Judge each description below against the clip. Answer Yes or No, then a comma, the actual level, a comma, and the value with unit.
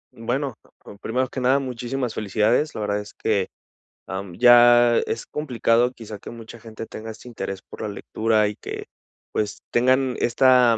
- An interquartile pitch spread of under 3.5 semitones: Yes, narrow, 2.6 semitones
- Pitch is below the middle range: Yes, low, 115 Hz